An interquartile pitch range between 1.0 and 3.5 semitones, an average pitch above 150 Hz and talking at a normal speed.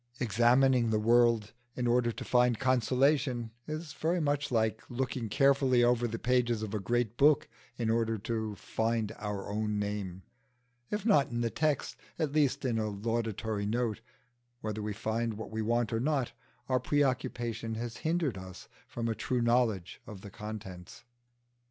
No: average, 2.8 semitones; low, 115 Hz; average, 165 wpm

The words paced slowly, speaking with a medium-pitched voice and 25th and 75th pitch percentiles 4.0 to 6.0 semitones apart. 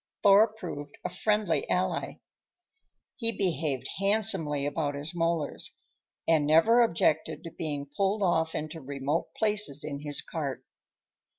Yes: slow, 125 wpm; medium, 165 Hz; average, 5.2 semitones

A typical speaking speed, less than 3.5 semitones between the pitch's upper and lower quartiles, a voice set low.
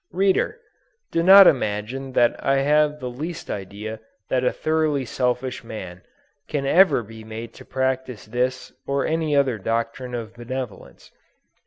No: average, 145 wpm; average, 4.2 semitones; low, 130 Hz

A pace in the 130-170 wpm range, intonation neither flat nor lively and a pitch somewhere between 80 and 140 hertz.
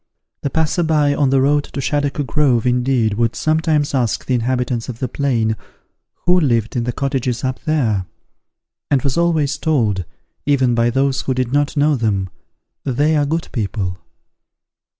Yes: average, 165 wpm; average, 3.7 semitones; low, 135 Hz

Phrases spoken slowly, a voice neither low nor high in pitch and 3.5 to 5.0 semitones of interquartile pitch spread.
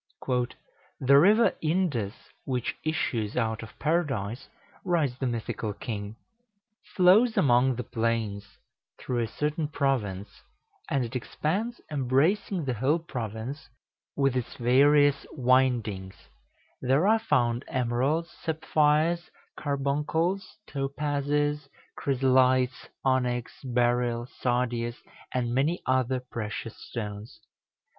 No: slow, 100 wpm; low, 130 Hz; average, 3.9 semitones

